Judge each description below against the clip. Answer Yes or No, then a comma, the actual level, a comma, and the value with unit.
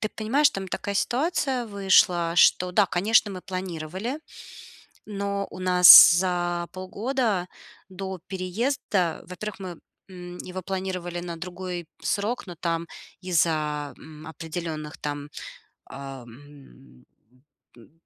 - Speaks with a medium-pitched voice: Yes, medium, 180 Hz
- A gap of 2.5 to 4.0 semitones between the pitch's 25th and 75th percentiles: Yes, average, 3.1 semitones